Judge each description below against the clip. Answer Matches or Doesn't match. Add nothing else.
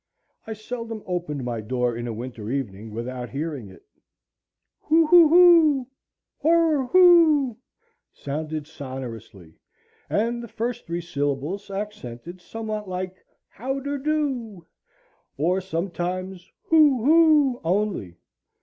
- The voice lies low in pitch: Doesn't match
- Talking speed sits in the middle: Doesn't match